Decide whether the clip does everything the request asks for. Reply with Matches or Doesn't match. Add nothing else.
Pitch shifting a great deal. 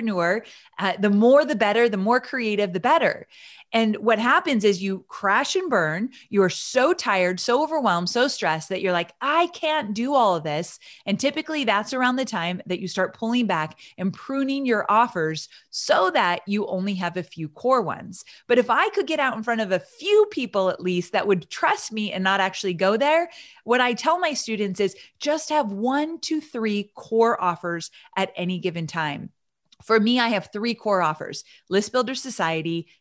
Matches